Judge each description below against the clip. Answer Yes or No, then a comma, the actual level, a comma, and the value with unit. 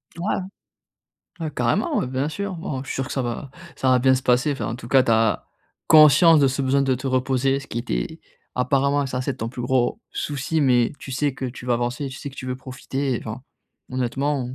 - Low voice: Yes, low, 130 Hz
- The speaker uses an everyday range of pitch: No, narrow, 1.9 semitones